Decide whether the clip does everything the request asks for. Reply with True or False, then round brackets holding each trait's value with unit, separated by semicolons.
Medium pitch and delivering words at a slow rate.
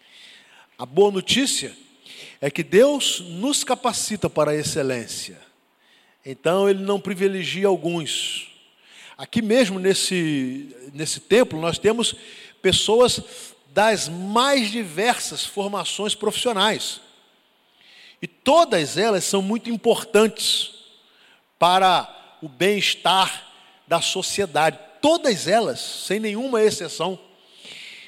False (200 Hz; 95 wpm)